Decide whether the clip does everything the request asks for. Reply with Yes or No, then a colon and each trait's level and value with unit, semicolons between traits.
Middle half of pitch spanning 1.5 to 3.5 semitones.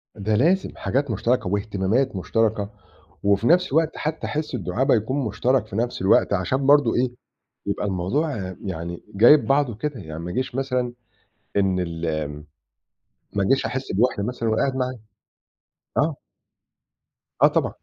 No: wide, 5.4 semitones